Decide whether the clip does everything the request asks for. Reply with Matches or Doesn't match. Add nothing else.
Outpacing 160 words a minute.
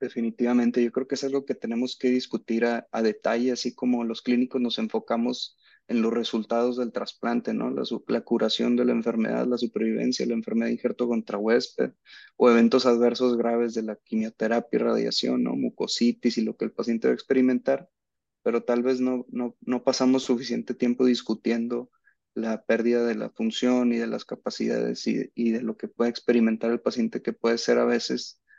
Matches